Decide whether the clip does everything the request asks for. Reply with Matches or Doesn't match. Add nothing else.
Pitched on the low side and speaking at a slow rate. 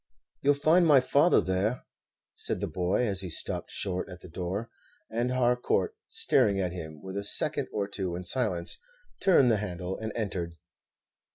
Doesn't match